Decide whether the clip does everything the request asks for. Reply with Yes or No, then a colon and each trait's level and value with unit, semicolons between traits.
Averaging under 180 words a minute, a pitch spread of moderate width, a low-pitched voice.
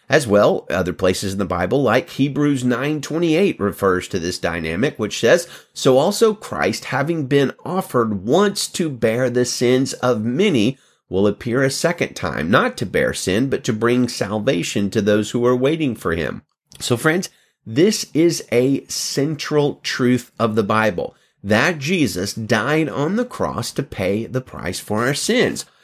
Yes: average, 165 wpm; average, 4.7 semitones; low, 130 Hz